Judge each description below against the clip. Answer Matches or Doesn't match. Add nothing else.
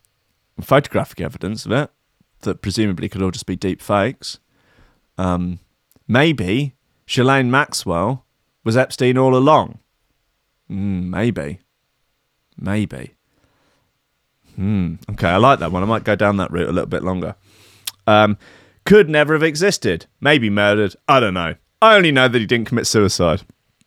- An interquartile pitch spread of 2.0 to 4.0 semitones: Doesn't match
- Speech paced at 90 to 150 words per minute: Matches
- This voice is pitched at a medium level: Doesn't match